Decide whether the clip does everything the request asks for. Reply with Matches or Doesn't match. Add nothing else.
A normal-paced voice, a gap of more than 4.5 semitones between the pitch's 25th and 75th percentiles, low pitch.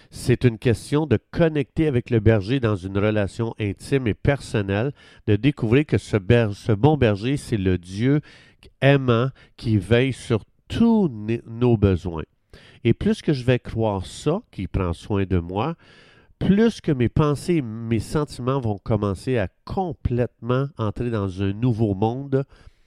Matches